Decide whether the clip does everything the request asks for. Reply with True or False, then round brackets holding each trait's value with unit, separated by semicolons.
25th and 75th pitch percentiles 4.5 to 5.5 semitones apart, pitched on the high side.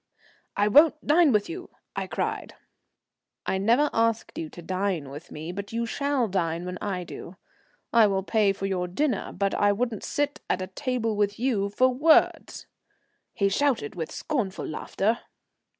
True (5.0 semitones; 205 Hz)